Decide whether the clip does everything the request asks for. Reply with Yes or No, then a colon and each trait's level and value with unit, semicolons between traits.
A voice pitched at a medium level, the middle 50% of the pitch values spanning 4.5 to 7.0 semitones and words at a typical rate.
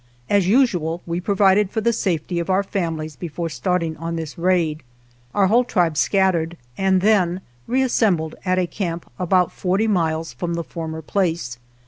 No: medium, 180 Hz; average, 3.0 semitones; average, 160 wpm